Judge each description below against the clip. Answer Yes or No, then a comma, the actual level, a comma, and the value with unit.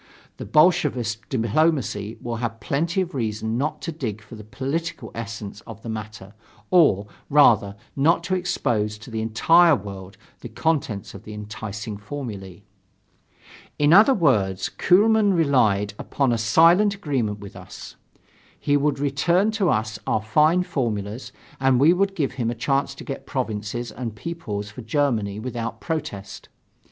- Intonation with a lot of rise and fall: Yes, wide, 6.4 semitones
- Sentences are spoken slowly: No, average, 155 wpm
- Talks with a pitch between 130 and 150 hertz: No, low, 120 Hz